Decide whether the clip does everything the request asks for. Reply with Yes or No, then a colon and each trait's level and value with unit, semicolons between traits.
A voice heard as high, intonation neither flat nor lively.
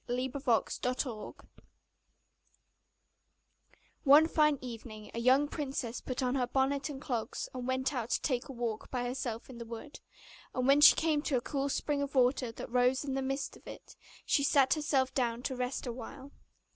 No: very high, 260 Hz; narrow, 2.3 semitones